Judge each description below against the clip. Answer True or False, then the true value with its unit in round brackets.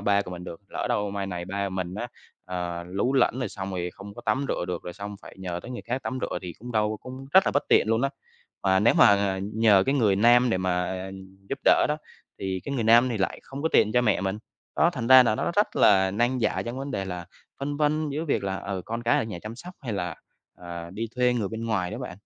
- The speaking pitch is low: True (105 Hz)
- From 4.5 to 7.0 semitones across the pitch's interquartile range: True (4.8 semitones)